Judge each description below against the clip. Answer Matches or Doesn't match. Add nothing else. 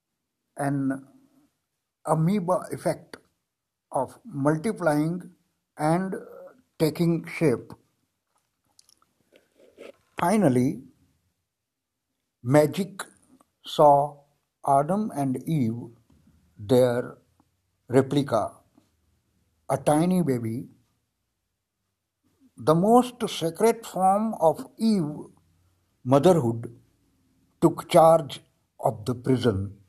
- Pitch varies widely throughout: Matches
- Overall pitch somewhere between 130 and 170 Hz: Matches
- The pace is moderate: Doesn't match